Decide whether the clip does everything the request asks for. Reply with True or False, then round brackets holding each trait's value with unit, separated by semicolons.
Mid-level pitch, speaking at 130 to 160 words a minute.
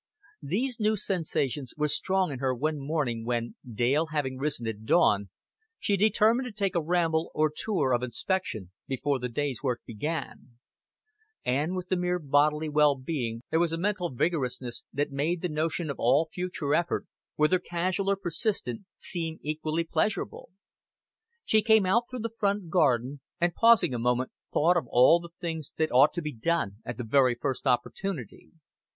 False (155 Hz; 170 wpm)